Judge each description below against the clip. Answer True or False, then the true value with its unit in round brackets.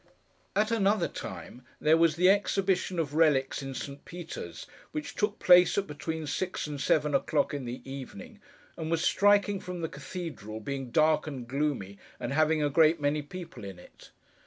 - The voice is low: False (155 Hz)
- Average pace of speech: True (175 wpm)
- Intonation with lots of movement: False (4.5 semitones)